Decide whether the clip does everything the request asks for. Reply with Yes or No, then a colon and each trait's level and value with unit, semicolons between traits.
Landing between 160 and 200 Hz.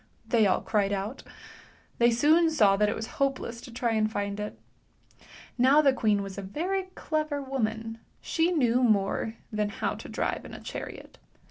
No: high, 230 Hz